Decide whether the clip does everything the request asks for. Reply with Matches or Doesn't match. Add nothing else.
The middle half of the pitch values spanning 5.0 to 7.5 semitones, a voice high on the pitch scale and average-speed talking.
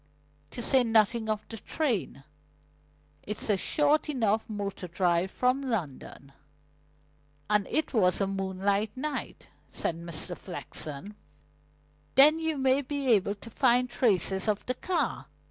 Doesn't match